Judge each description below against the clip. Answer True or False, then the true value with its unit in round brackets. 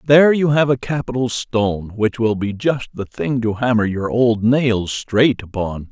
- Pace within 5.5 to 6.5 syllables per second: False (4.5 syllables/s)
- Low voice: True (115 Hz)